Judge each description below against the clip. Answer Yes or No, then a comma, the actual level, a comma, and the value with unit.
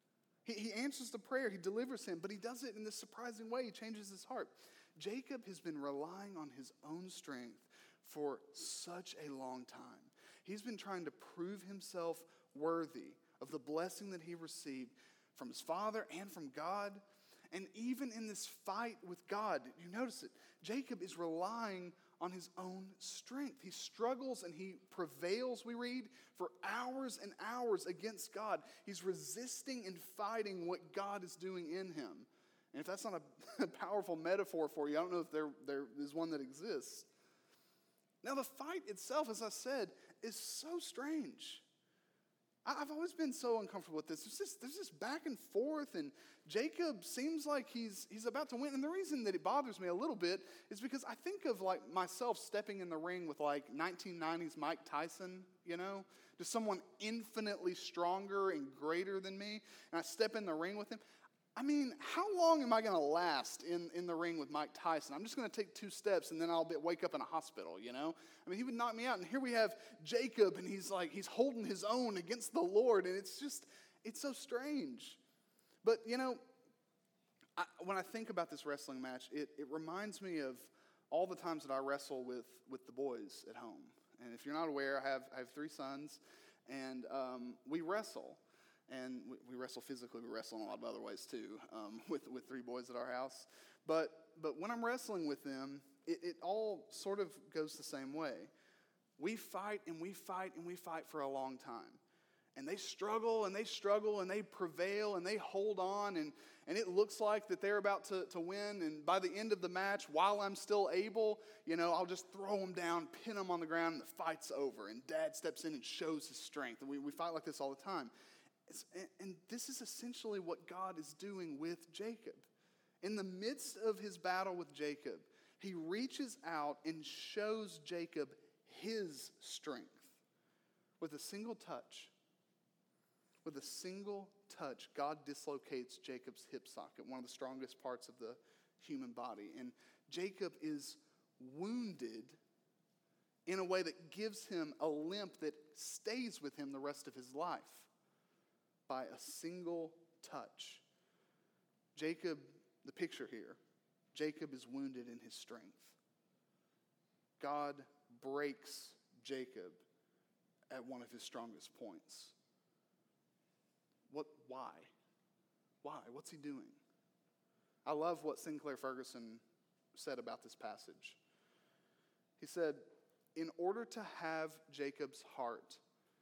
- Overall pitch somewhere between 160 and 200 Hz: Yes, high, 190 Hz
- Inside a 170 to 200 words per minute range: Yes, average, 180 wpm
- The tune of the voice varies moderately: No, wide, 6.5 semitones